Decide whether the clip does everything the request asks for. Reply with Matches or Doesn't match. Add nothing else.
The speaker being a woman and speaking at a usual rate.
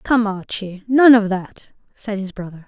Matches